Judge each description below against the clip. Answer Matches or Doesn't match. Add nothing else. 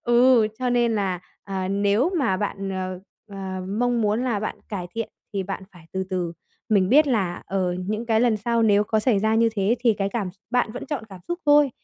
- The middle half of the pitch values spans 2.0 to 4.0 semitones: Matches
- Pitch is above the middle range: Matches